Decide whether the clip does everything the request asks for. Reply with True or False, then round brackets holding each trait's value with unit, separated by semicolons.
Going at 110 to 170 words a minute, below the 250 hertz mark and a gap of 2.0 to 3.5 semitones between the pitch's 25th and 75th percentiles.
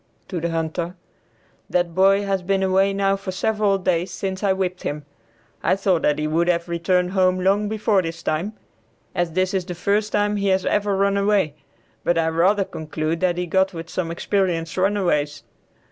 False (190 wpm; 185 Hz; 2.8 semitones)